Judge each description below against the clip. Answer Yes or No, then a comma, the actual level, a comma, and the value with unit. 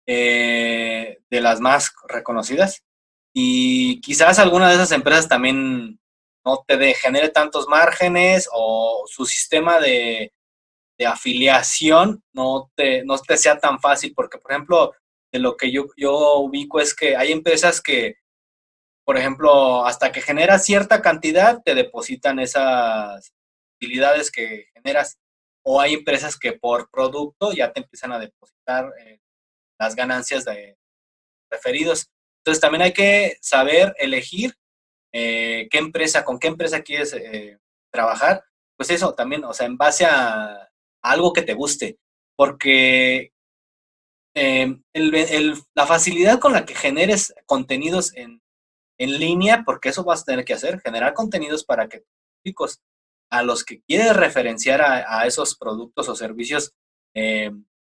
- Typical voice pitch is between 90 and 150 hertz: Yes, medium, 140 Hz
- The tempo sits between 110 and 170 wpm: Yes, average, 145 wpm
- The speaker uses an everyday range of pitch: No, wide, 7.3 semitones